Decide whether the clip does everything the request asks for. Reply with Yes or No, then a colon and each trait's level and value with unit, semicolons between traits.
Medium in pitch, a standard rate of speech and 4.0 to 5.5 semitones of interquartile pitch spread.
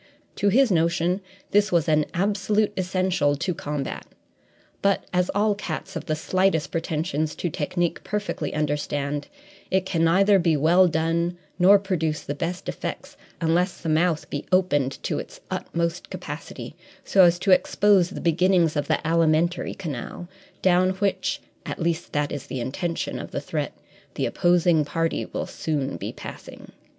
No: medium, 170 Hz; average, 155 wpm; average, 3.1 semitones